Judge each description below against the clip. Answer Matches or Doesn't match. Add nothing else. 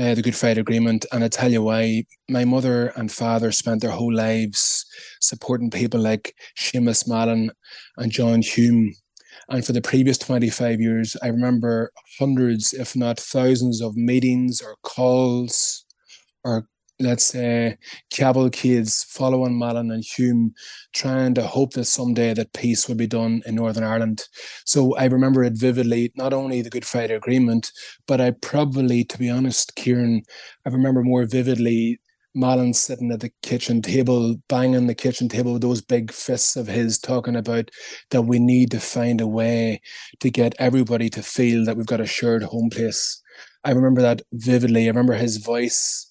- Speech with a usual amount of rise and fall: Doesn't match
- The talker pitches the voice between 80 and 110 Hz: Doesn't match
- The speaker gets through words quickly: Doesn't match